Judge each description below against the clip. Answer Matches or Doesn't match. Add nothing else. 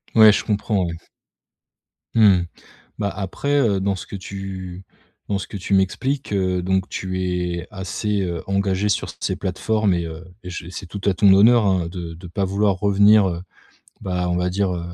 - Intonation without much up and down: Matches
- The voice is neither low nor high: Doesn't match